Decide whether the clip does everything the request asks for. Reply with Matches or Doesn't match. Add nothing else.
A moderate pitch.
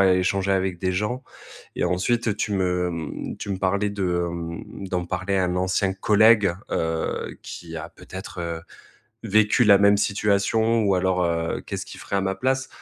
Doesn't match